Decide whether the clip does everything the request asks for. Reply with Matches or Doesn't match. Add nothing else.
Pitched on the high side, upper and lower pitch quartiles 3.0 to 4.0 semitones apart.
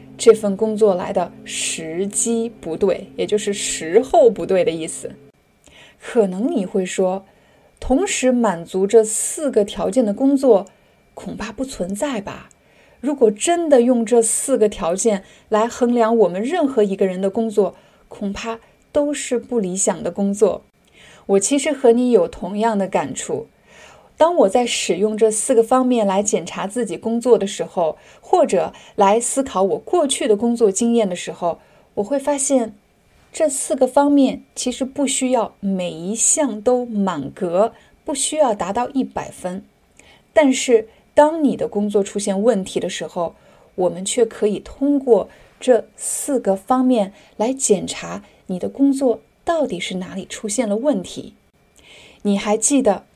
Doesn't match